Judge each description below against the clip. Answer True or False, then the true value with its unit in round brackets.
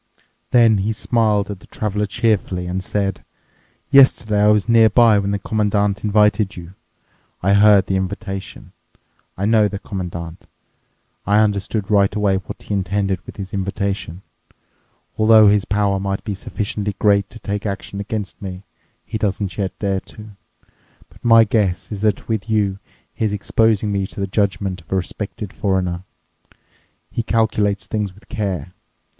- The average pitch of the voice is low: True (100 Hz)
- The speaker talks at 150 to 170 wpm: True (155 wpm)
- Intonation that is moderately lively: False (1.7 semitones)